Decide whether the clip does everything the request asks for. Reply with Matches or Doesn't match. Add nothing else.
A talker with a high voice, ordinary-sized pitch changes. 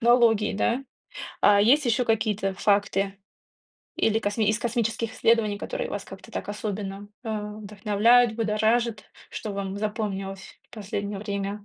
Doesn't match